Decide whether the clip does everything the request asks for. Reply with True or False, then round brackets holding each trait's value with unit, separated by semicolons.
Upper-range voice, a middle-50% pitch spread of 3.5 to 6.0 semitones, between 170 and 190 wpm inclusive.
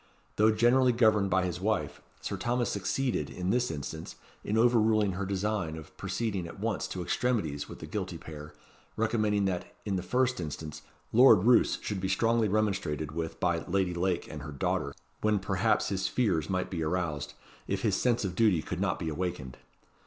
False (95 Hz; 4.6 semitones; 185 wpm)